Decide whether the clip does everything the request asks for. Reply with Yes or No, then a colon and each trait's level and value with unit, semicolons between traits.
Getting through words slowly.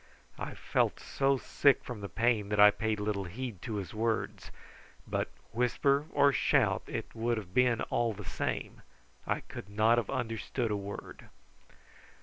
No: average, 160 wpm